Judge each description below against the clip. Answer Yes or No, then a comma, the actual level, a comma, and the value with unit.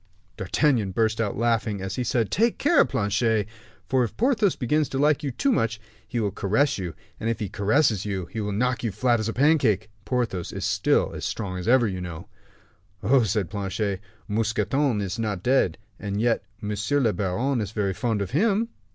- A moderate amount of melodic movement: Yes, average, 4.2 semitones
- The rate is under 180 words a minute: No, average, 200 wpm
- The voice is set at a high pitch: No, low, 110 Hz